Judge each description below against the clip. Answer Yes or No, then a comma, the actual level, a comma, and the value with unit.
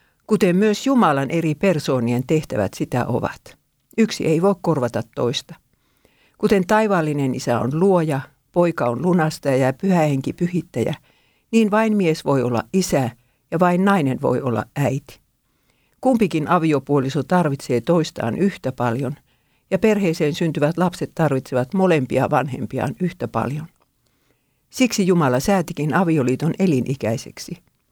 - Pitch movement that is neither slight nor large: No, wide, 5.8 semitones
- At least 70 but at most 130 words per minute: Yes, average, 125 wpm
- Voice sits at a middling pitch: Yes, medium, 155 Hz